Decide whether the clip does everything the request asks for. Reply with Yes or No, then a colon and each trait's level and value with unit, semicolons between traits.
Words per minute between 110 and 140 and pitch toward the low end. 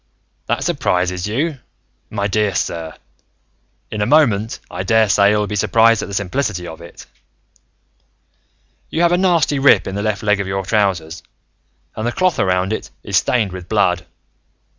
No: average, 160 wpm; low, 105 Hz